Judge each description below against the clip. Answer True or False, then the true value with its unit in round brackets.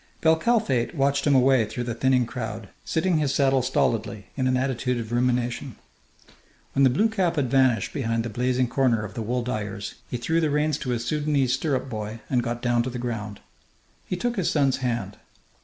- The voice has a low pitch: True (125 Hz)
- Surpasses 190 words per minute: True (200 wpm)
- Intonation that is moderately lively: True (3.1 semitones)